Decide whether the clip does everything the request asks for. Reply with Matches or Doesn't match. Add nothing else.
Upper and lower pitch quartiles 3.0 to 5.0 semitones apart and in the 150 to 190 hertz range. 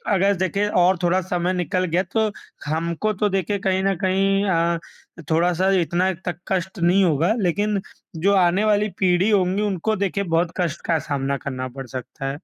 Doesn't match